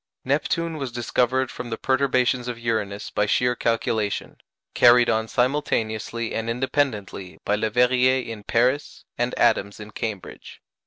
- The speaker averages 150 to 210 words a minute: No, slow, 135 wpm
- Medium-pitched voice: No, low, 120 Hz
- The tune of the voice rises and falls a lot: No, average, 2.8 semitones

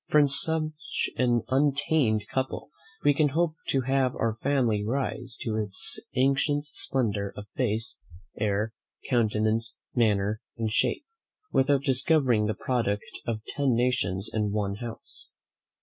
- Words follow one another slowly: Yes, slow, 130 wpm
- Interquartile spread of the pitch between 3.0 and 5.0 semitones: Yes, average, 4.2 semitones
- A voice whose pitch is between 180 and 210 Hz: No, low, 120 Hz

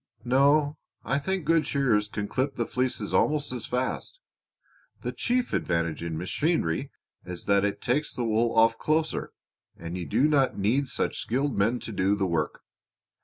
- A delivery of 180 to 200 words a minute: No, average, 170 wpm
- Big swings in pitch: Yes, wide, 6.2 semitones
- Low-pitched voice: Yes, low, 120 Hz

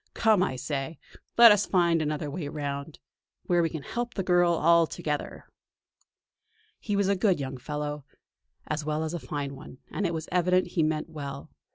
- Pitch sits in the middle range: Yes, medium, 160 Hz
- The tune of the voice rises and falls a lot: No, average, 3.5 semitones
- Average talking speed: Yes, average, 185 wpm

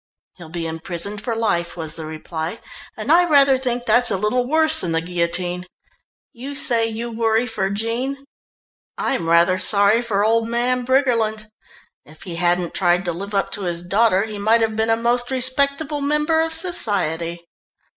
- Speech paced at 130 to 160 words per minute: No, average, 175 wpm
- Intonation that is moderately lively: No, wide, 6.0 semitones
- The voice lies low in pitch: No, high, 220 Hz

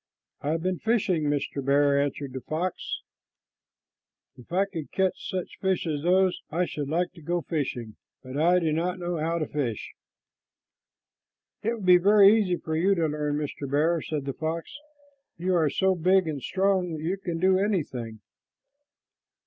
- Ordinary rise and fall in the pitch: Yes, average, 4.0 semitones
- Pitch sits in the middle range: Yes, medium, 165 Hz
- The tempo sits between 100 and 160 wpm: No, average, 175 wpm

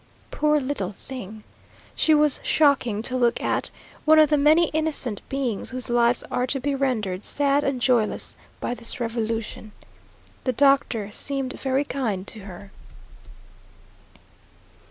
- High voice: Yes, very high, 255 Hz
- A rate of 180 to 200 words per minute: No, slow, 135 wpm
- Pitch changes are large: No, average, 4.0 semitones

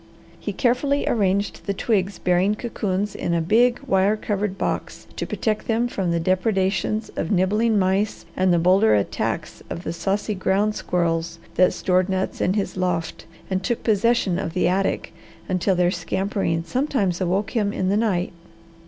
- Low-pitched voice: No, high, 190 Hz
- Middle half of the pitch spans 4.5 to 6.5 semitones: No, average, 2.7 semitones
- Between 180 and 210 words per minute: No, average, 165 wpm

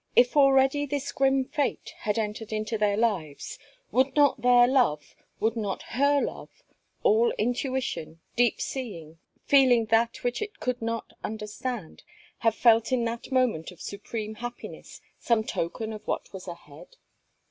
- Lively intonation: No, average, 3.8 semitones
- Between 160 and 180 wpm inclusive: No, average, 145 wpm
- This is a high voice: Yes, high, 235 Hz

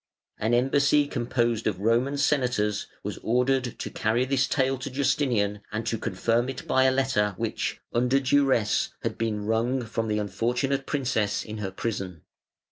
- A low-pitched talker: Yes, low, 120 Hz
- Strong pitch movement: No, average, 3.7 semitones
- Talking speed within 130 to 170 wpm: Yes, average, 160 wpm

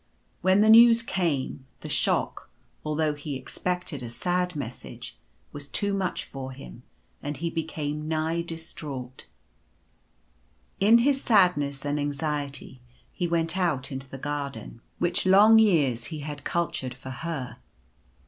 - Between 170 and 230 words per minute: No, average, 150 wpm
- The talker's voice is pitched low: No, medium, 150 Hz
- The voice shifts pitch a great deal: No, average, 4.6 semitones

